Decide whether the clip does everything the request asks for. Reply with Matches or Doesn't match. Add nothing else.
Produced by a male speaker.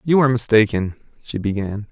Matches